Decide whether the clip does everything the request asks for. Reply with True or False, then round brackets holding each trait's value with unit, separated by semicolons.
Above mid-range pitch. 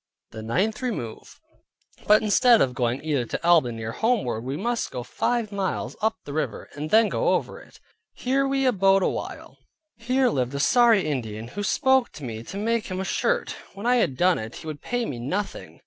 True (195 Hz)